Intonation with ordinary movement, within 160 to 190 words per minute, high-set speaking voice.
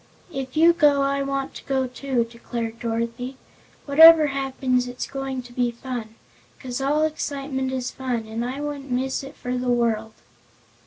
No: narrow, 2.2 semitones; average, 165 wpm; very high, 260 Hz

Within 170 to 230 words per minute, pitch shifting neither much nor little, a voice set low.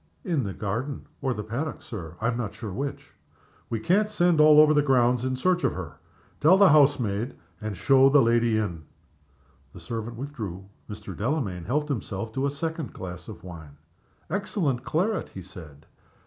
No: average, 180 wpm; wide, 6.8 semitones; low, 120 Hz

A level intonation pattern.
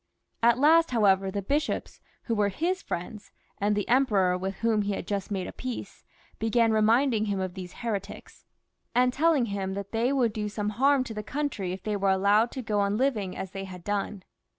No: average, 3.8 semitones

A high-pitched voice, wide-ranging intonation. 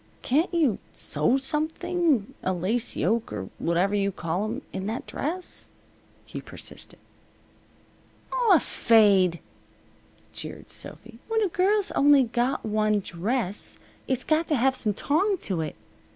Yes: high, 235 Hz; wide, 7.8 semitones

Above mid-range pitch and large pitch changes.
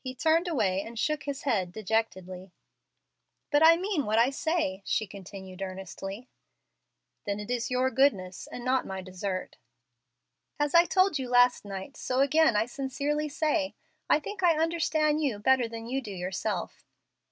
Yes: very high, 250 Hz; wide, 7.1 semitones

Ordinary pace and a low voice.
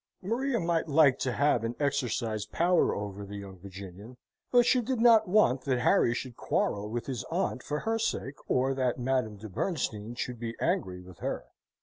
Yes: average, 190 wpm; low, 130 Hz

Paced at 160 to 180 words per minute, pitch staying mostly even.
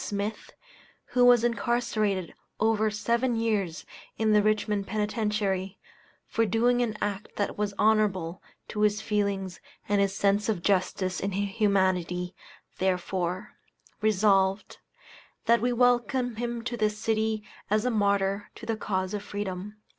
No: slow, 135 wpm; narrow, 2.3 semitones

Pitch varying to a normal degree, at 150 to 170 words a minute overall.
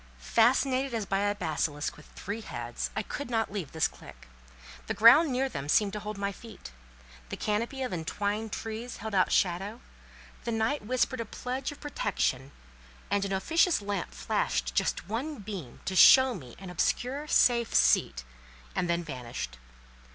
No: wide, 6.1 semitones; average, 165 wpm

